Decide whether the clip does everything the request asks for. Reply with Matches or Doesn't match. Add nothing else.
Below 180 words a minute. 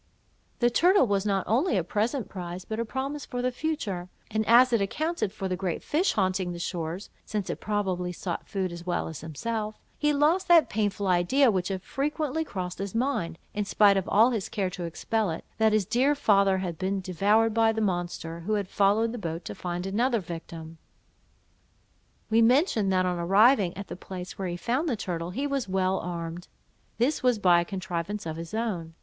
Doesn't match